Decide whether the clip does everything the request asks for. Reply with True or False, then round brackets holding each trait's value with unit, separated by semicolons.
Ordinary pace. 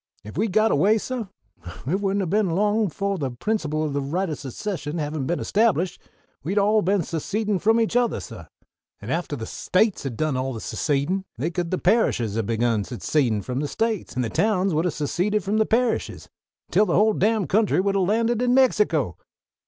False (210 wpm)